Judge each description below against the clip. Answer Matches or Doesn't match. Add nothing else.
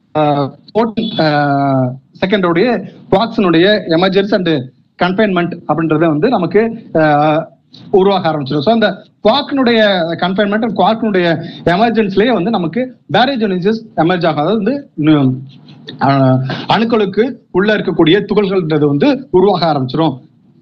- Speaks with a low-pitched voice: Doesn't match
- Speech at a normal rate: Matches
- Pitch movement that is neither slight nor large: Doesn't match